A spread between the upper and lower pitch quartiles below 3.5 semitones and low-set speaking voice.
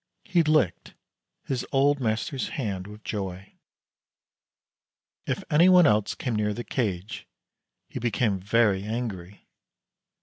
No: average, 5.2 semitones; low, 110 Hz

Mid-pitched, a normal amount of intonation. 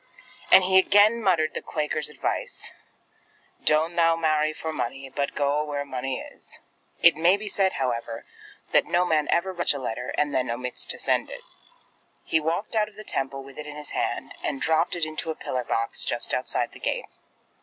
Yes: medium, 155 Hz; average, 4.0 semitones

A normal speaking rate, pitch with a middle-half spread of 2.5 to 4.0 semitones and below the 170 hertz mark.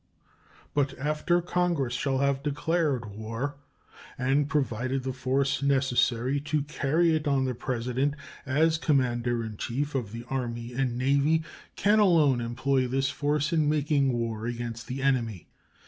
Yes: average, 145 wpm; average, 3.4 semitones; low, 135 Hz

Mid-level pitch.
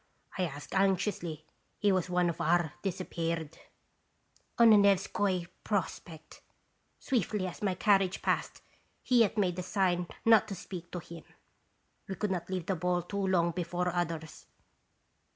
Yes: medium, 180 Hz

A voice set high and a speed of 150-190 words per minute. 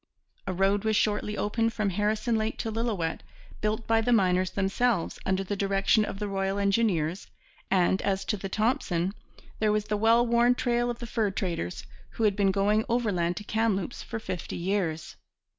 Yes: high, 205 Hz; average, 180 wpm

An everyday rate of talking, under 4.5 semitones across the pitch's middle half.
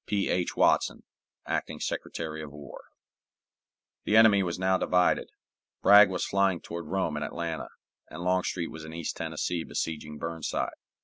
Yes: average, 145 wpm; average, 3.0 semitones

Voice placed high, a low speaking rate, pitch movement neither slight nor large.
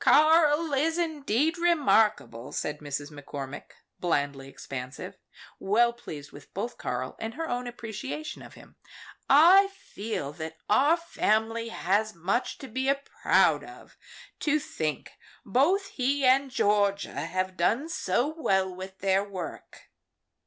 No: high, 220 Hz; slow, 130 wpm; wide, 8.5 semitones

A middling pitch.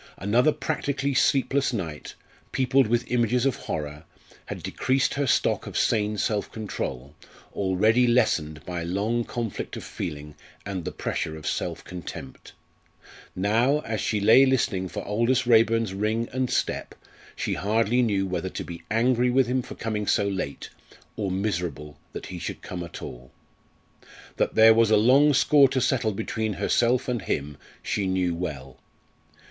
No: low, 110 Hz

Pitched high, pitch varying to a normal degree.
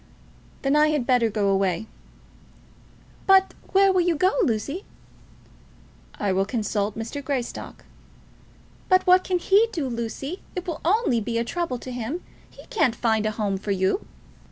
No: very high, 255 Hz; wide, 8.6 semitones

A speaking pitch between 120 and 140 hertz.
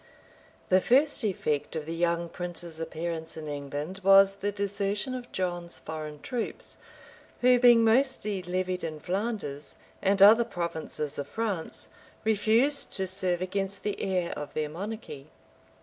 No: medium, 185 Hz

